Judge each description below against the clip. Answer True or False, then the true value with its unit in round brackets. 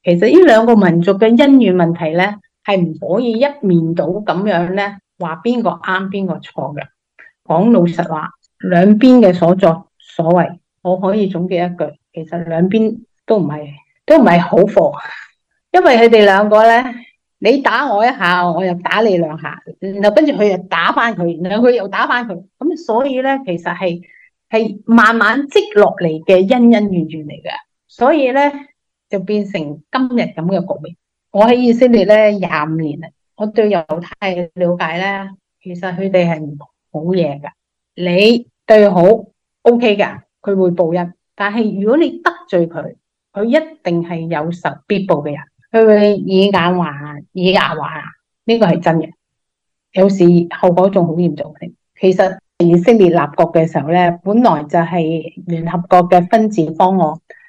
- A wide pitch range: False (4.4 semitones)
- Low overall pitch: False (185 Hz)